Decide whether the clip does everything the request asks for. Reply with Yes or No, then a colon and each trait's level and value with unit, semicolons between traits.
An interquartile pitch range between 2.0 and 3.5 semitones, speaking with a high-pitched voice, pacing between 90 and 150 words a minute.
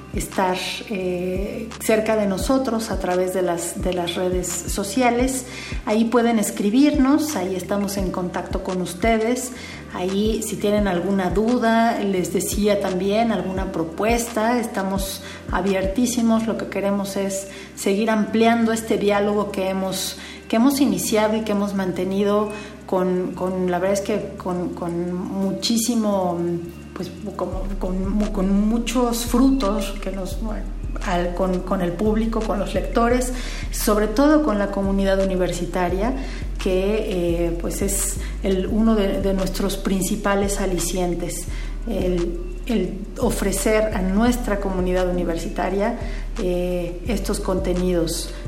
Yes: average, 3.0 semitones; high, 195 Hz; average, 130 wpm